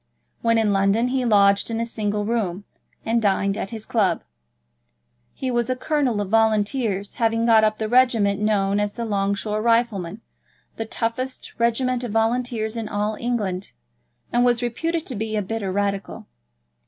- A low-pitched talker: No, high, 220 Hz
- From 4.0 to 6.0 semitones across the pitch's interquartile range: No, average, 2.7 semitones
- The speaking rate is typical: Yes, average, 165 wpm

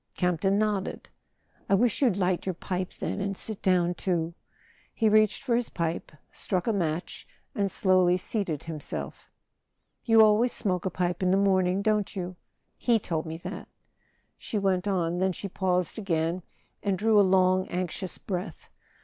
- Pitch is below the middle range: No, medium, 185 Hz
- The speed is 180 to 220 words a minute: No, average, 165 wpm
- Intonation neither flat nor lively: No, narrow, 2.3 semitones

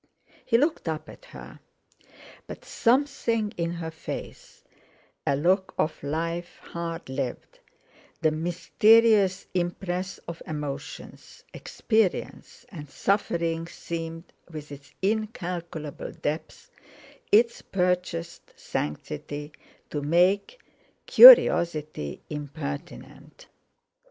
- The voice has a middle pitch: Yes, medium, 170 Hz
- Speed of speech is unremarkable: No, slow, 85 wpm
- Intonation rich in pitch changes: No, average, 4.2 semitones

